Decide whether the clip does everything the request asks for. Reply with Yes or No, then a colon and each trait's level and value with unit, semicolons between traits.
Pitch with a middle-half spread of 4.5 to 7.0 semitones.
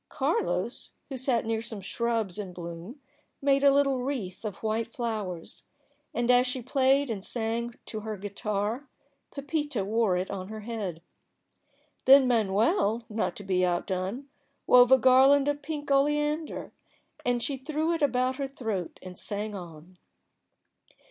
Yes: average, 5.2 semitones